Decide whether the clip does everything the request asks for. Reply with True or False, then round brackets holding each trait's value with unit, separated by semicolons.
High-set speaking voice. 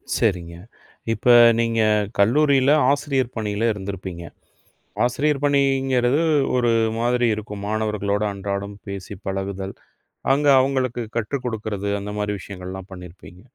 False (105 Hz)